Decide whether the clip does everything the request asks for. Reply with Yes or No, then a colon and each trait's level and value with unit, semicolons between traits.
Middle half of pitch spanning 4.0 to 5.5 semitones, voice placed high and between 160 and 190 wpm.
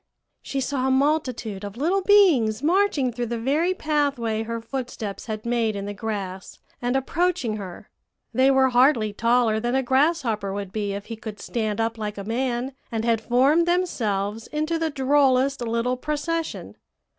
Yes: average, 4.6 semitones; high, 245 Hz; average, 170 wpm